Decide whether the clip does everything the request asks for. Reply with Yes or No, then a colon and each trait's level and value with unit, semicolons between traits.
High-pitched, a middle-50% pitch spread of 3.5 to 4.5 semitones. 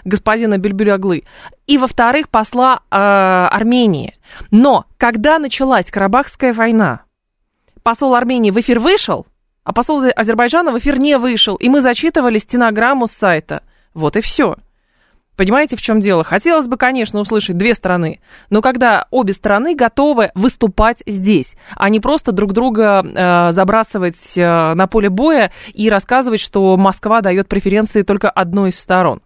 Yes: high, 220 Hz; average, 4.1 semitones